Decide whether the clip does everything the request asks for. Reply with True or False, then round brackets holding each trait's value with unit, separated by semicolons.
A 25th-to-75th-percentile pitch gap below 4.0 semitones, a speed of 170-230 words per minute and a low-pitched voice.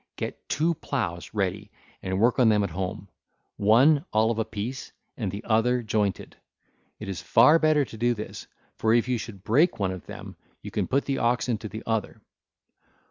True (3.4 semitones; 190 wpm; 110 Hz)